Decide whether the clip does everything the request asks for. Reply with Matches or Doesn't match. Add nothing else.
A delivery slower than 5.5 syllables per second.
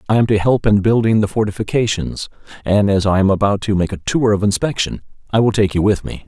Doesn't match